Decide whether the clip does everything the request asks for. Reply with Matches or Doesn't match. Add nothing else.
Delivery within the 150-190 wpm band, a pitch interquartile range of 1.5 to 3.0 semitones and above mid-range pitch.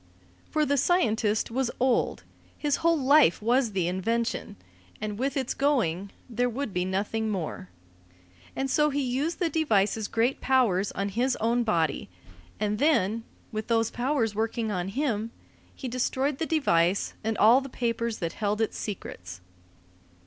Doesn't match